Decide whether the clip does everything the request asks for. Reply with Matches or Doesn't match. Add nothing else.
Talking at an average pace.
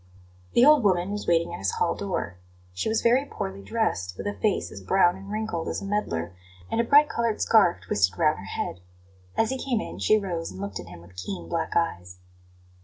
Doesn't match